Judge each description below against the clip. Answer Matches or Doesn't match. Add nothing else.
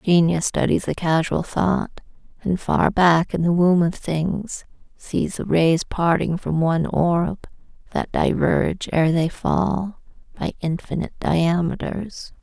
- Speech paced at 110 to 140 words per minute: Matches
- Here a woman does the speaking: Matches